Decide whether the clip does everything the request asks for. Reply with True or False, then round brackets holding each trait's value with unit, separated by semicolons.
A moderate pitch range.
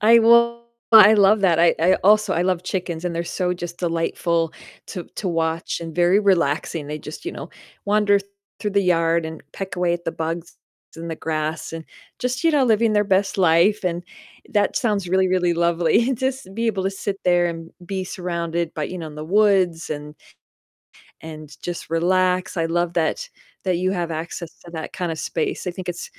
True (3.1 semitones)